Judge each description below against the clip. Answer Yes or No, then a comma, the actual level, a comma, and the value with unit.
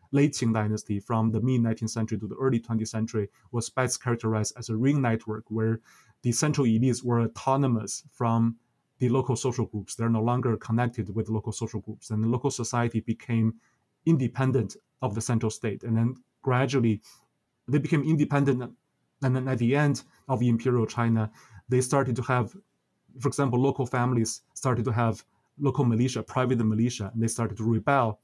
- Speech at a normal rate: Yes, average, 175 wpm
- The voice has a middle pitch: No, low, 120 Hz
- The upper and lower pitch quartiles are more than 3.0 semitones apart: No, narrow, 2.5 semitones